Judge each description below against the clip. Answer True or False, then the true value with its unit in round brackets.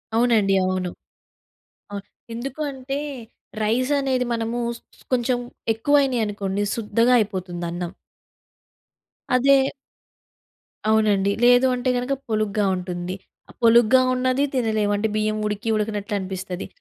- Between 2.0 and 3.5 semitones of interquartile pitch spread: False (3.9 semitones)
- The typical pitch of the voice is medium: False (220 Hz)